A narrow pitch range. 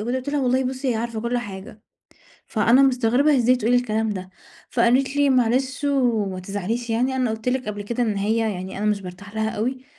No: average, 3.3 semitones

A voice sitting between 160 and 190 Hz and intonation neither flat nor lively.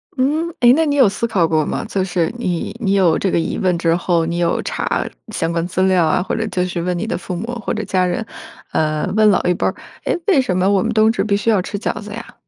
Yes: medium, 185 Hz; average, 4.1 semitones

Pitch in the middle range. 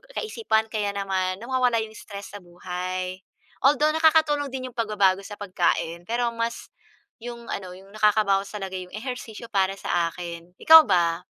No: high, 205 Hz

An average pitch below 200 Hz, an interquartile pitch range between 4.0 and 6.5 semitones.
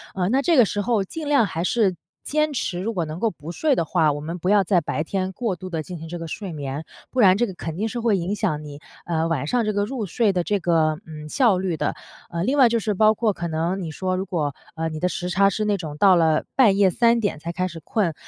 Yes: medium, 185 Hz; average, 4.7 semitones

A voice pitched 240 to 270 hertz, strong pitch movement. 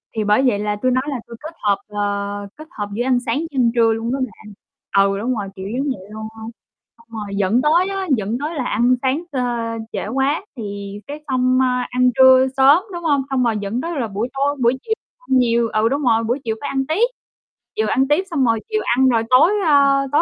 No: very high, 250 Hz; average, 4.2 semitones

